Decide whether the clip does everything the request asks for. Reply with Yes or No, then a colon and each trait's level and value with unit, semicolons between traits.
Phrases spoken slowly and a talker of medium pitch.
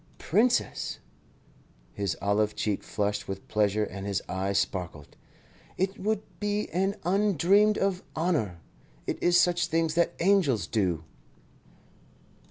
Yes: slow, 120 wpm; medium, 160 Hz